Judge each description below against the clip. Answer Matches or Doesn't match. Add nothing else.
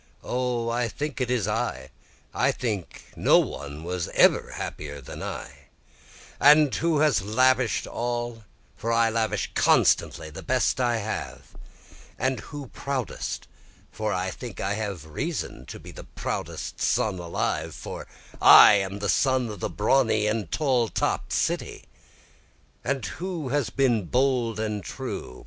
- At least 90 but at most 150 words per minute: Matches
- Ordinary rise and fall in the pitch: Matches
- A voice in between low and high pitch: Doesn't match